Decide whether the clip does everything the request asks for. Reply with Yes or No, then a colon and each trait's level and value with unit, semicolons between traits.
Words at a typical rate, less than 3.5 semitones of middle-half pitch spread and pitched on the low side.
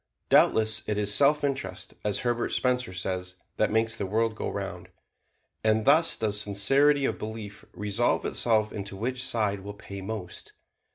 Yes: average, 160 wpm; average, 3.1 semitones; low, 110 Hz